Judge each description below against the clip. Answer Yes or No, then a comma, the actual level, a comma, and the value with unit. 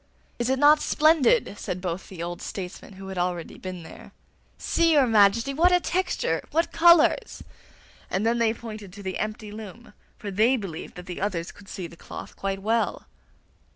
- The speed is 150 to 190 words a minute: Yes, average, 185 wpm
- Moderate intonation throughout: No, wide, 6.0 semitones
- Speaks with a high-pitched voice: Yes, high, 210 Hz